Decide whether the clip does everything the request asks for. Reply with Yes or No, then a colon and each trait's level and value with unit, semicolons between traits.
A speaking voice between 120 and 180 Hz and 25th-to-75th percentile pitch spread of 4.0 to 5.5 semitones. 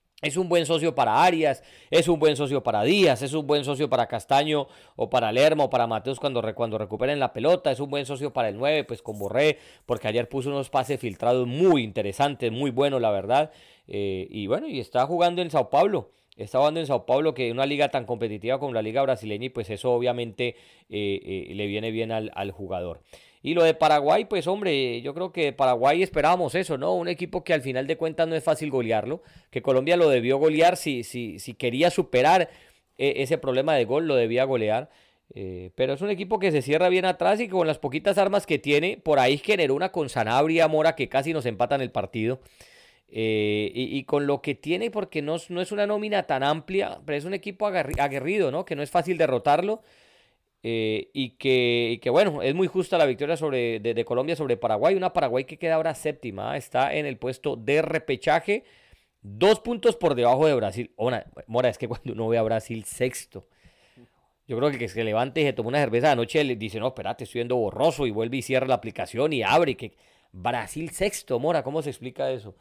Yes: medium, 140 Hz; average, 5.2 semitones